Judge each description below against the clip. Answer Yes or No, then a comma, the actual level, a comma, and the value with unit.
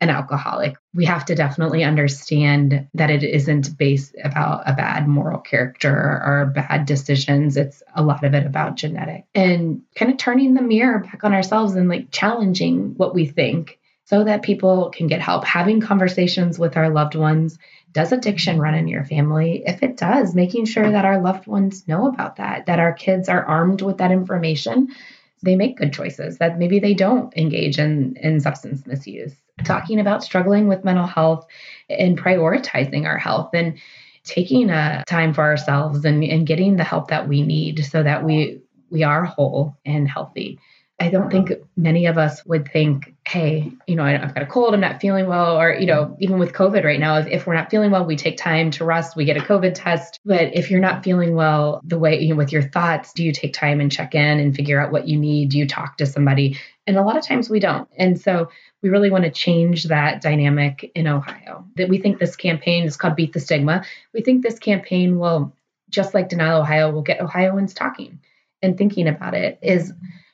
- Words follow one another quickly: Yes, fast, 210 wpm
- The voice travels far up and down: No, average, 3.8 semitones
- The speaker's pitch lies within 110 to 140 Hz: No, medium, 165 Hz